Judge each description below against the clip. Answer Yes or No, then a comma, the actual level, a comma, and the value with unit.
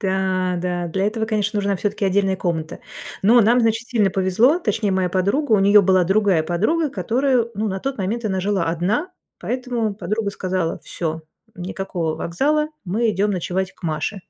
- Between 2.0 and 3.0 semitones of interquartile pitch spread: No, average, 3.4 semitones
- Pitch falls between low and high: No, high, 200 Hz